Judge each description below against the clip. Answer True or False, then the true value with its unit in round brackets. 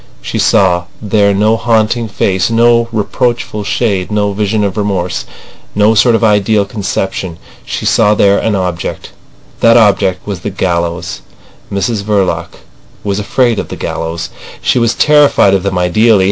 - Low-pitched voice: True (105 Hz)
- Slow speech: False (150 wpm)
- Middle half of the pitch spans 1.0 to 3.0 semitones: True (2.7 semitones)